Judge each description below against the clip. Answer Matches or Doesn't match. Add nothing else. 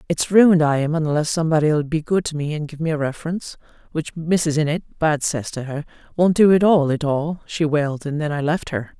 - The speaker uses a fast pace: Matches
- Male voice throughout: Doesn't match